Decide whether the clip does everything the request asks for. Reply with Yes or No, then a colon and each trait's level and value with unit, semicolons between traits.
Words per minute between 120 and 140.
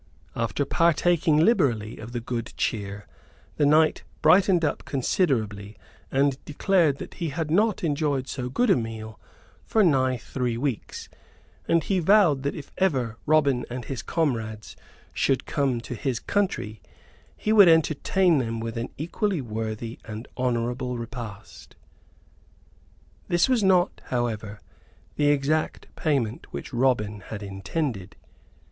Yes: slow, 135 wpm